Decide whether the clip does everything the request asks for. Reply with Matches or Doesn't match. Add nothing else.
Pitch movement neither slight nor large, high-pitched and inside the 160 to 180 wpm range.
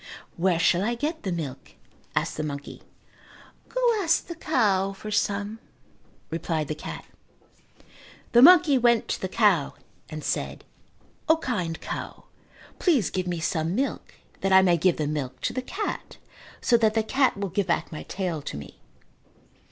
Doesn't match